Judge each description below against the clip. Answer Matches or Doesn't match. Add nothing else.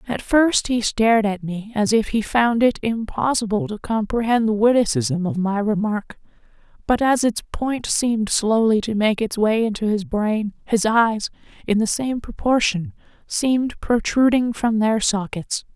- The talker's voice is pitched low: Doesn't match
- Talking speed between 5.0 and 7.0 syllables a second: Doesn't match